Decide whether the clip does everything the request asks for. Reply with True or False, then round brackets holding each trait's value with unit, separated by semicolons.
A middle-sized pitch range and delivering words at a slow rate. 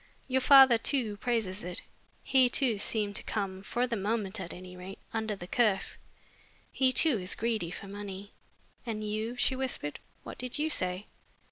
False (4.3 semitones; 170 wpm)